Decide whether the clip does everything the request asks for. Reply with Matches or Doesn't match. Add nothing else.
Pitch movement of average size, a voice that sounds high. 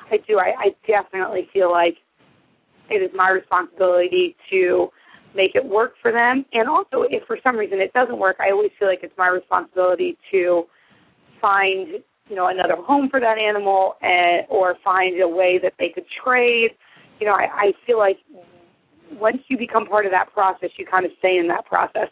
Matches